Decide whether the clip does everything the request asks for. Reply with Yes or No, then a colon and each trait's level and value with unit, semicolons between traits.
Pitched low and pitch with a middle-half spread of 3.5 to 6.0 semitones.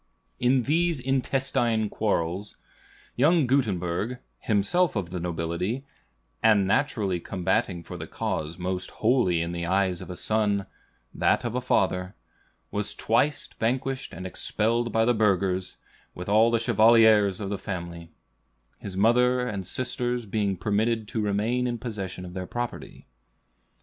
Yes: low, 105 Hz; average, 4.6 semitones